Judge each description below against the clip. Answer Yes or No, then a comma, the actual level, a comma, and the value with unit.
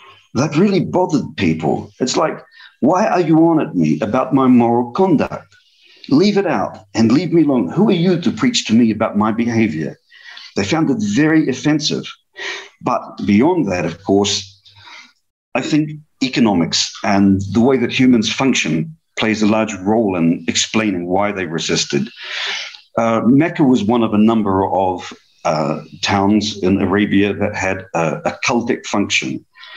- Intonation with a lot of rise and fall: Yes, wide, 7.8 semitones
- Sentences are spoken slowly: No, average, 160 wpm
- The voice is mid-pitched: No, low, 110 Hz